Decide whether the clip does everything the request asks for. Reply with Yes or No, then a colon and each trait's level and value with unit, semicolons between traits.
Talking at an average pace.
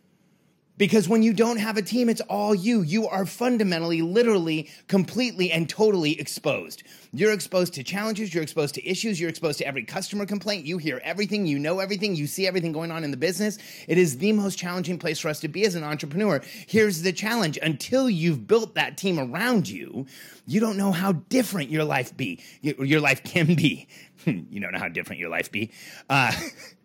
No: fast, 220 wpm